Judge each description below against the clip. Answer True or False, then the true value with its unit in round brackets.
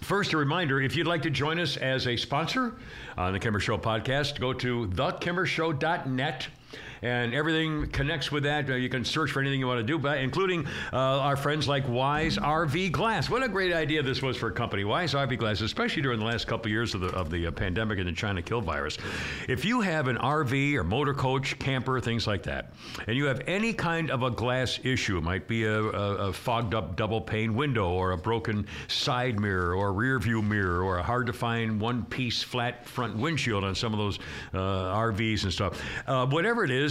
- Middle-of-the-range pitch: False (125 Hz)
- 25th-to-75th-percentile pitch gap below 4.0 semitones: False (5.0 semitones)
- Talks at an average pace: False (220 wpm)